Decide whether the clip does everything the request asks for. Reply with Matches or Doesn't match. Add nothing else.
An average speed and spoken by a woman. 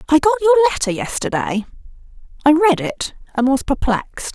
Matches